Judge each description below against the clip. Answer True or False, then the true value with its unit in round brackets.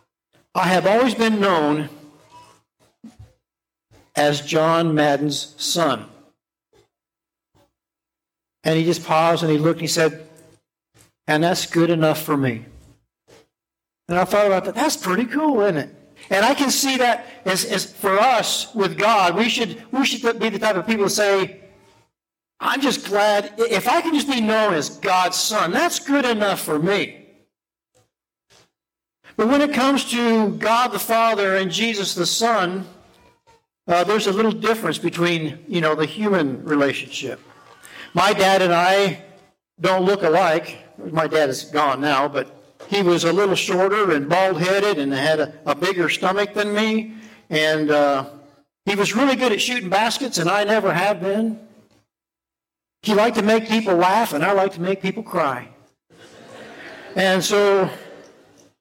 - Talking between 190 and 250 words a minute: False (160 wpm)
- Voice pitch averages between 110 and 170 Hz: False (190 Hz)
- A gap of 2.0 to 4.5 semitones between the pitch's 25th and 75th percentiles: False (5.3 semitones)